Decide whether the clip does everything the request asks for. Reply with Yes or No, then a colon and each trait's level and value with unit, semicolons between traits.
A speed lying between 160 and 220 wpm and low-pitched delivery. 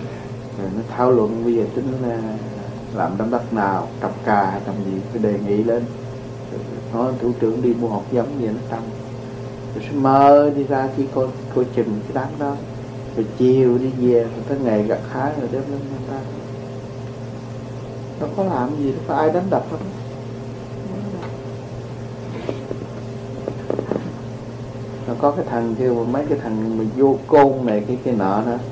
Yes: average, 170 wpm; low, 125 Hz